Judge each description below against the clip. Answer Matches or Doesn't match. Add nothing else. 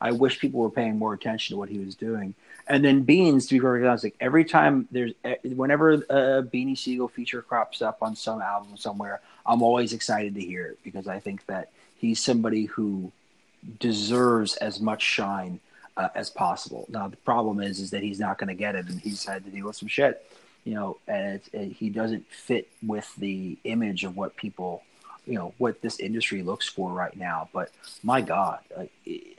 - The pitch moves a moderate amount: Matches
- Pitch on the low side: Matches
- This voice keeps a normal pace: Doesn't match